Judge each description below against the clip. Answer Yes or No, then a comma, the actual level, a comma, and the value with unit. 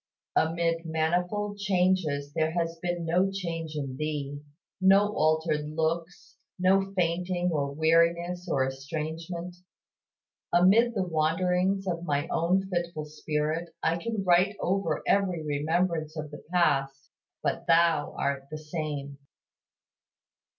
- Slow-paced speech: Yes, slow, 120 wpm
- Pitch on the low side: No, medium, 165 Hz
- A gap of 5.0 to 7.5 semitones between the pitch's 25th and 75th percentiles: No, average, 2.7 semitones